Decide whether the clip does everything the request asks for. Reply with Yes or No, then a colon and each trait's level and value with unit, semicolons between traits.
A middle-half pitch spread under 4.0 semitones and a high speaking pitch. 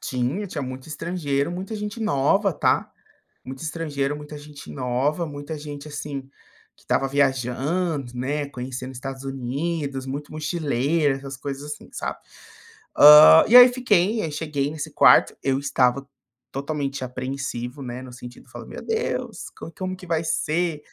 No: average, 3.2 semitones; medium, 145 Hz